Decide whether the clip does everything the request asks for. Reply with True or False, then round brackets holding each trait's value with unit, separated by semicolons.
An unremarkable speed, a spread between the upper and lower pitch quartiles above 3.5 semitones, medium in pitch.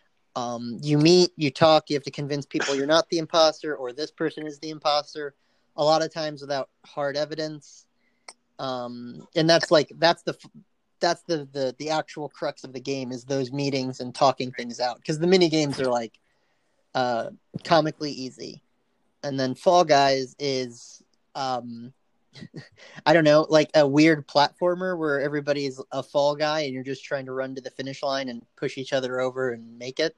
False (185 wpm; 3.1 semitones; 145 Hz)